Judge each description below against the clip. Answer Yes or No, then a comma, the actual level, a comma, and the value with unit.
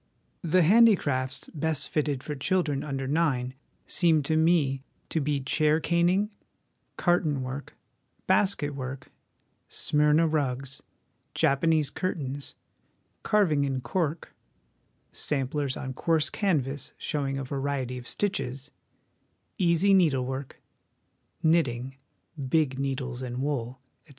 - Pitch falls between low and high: Yes, medium, 145 Hz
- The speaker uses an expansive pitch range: No, average, 3.6 semitones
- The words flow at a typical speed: No, slow, 110 wpm